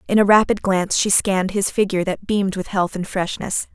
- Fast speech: Yes, fast, 225 wpm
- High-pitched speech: Yes, high, 195 Hz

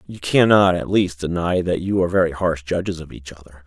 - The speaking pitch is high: No, very low, 85 Hz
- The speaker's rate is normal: No, fast, 230 wpm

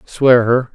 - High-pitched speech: No, low, 125 Hz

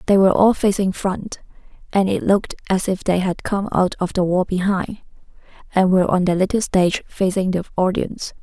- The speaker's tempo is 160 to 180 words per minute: No, average, 190 wpm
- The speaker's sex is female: Yes, female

